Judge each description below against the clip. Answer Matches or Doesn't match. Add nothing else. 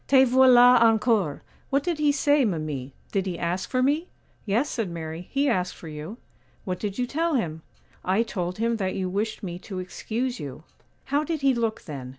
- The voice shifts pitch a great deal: Matches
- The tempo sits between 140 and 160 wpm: Doesn't match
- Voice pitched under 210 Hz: Doesn't match